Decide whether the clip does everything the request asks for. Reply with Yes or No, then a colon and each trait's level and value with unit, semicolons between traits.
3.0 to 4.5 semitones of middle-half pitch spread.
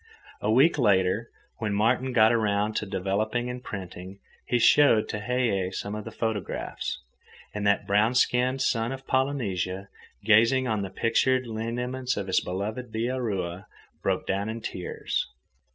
Yes: average, 3.7 semitones